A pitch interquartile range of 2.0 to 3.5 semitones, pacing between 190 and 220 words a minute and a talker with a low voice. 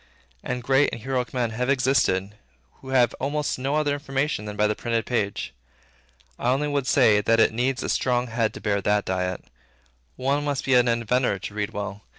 No: average, 4.3 semitones; average, 195 wpm; low, 125 Hz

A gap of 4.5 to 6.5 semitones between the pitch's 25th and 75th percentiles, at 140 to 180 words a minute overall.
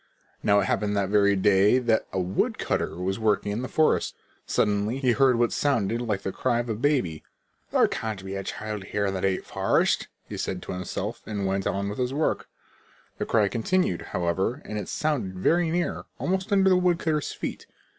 No: average, 5.0 semitones; average, 195 wpm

